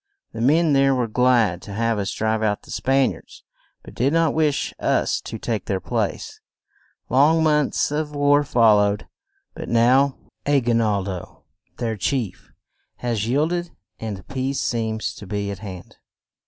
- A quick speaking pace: No, average, 170 wpm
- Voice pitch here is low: Yes, low, 120 Hz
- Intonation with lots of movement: No, average, 4.9 semitones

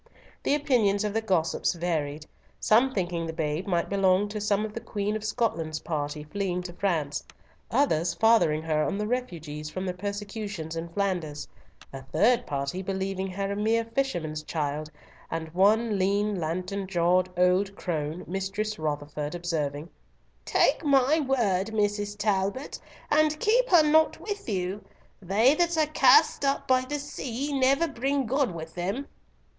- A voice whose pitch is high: Yes, high, 195 Hz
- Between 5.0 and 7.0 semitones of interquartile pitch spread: Yes, wide, 5.6 semitones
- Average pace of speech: Yes, average, 155 wpm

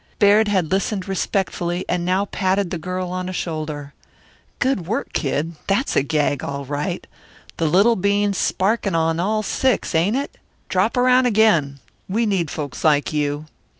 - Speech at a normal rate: Yes, average, 160 wpm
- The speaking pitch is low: No, medium, 185 Hz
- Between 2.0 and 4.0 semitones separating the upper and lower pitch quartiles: No, average, 4.6 semitones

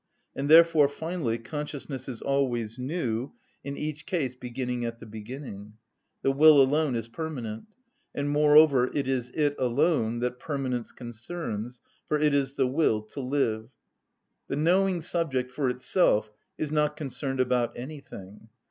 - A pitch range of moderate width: Yes, average, 3.9 semitones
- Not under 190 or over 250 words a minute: No, average, 145 wpm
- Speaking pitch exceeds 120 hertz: Yes, low, 135 Hz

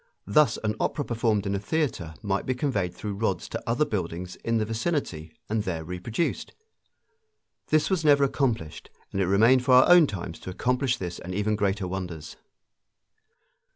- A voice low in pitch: Yes, low, 105 Hz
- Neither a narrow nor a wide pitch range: No, wide, 5.8 semitones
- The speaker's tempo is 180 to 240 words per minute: No, average, 170 wpm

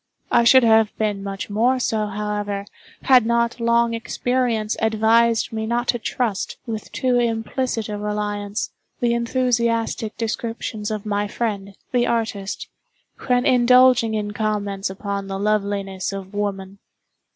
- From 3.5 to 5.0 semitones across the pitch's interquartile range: No, narrow, 2.4 semitones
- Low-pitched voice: No, high, 220 Hz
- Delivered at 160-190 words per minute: No, slow, 135 wpm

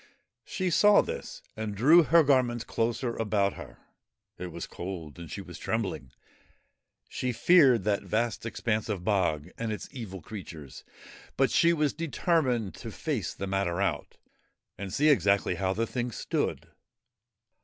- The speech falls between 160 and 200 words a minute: No, average, 150 wpm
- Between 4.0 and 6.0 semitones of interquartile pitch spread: Yes, average, 5.2 semitones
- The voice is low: Yes, low, 110 Hz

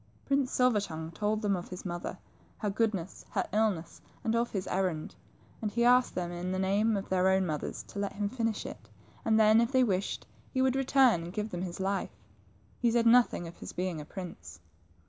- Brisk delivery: Yes, fast, 215 wpm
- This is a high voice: Yes, high, 200 Hz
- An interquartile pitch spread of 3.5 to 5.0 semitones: Yes, average, 4.0 semitones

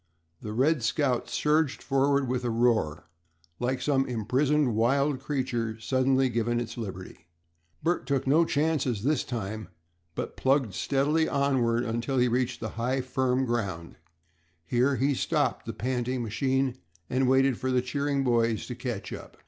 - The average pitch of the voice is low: Yes, low, 125 Hz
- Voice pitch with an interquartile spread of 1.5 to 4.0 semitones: Yes, average, 2.7 semitones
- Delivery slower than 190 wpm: Yes, average, 150 wpm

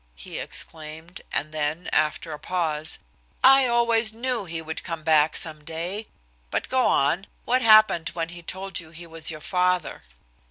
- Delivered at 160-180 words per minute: Yes, average, 165 wpm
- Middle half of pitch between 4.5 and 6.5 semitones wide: Yes, average, 5.1 semitones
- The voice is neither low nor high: Yes, medium, 170 Hz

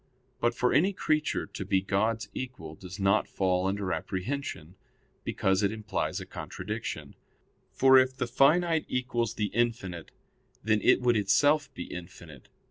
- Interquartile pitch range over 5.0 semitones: Yes, wide, 5.4 semitones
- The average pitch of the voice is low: Yes, low, 110 Hz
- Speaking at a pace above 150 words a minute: No, average, 145 wpm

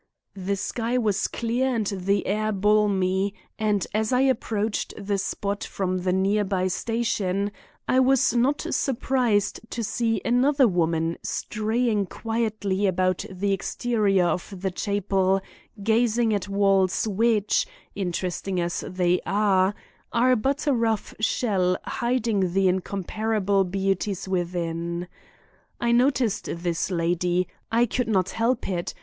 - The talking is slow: Yes, slow, 130 wpm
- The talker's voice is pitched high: Yes, high, 200 Hz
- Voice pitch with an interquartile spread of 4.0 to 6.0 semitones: No, average, 3.5 semitones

